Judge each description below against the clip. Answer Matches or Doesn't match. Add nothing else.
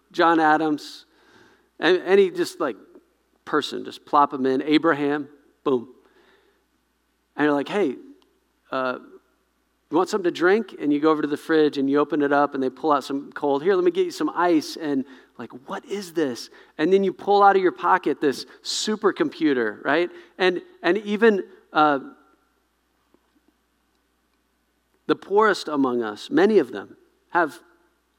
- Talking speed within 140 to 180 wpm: Matches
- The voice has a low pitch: Doesn't match